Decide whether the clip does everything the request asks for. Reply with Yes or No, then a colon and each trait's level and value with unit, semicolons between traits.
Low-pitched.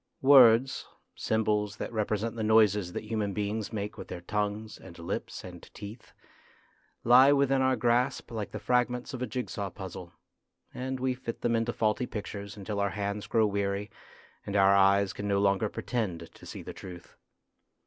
Yes: low, 105 Hz